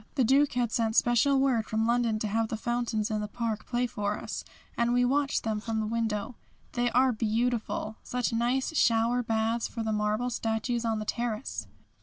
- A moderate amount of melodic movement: No, narrow, 1.9 semitones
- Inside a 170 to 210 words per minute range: Yes, average, 195 wpm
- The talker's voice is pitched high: Yes, high, 230 Hz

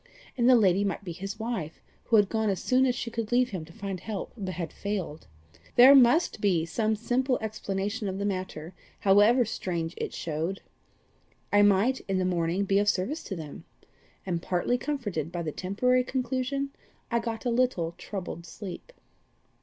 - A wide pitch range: No, average, 4.8 semitones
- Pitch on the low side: No, high, 205 Hz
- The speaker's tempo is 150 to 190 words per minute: Yes, average, 180 wpm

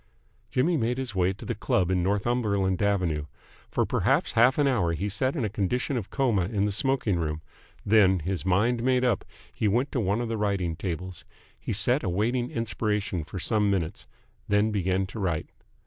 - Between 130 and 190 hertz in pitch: No, low, 105 Hz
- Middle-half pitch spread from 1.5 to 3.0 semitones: No, average, 4.3 semitones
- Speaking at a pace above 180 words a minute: Yes, average, 190 wpm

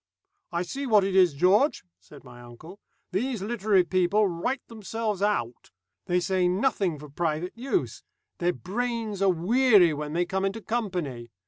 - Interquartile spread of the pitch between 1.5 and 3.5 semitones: No, average, 4.3 semitones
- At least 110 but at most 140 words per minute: No, average, 155 wpm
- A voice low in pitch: No, high, 190 Hz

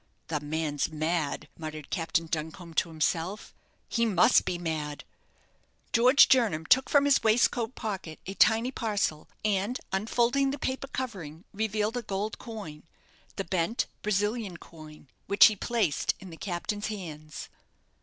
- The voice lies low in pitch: No, high, 195 Hz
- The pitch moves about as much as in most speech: No, wide, 5.9 semitones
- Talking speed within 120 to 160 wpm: Yes, average, 140 wpm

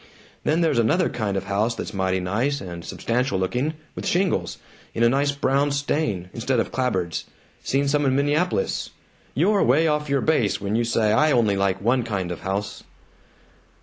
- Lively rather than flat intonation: Yes, wide, 6.4 semitones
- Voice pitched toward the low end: Yes, low, 120 Hz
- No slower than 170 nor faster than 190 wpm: Yes, average, 180 wpm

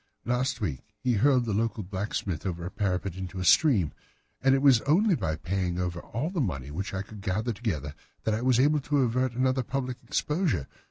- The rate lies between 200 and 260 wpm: Yes, fast, 205 wpm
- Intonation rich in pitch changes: Yes, wide, 6.0 semitones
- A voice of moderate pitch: No, low, 110 Hz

